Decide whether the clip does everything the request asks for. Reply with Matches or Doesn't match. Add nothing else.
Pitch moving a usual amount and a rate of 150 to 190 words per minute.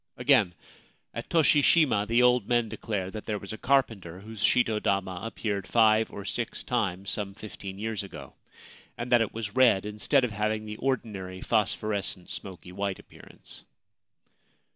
Matches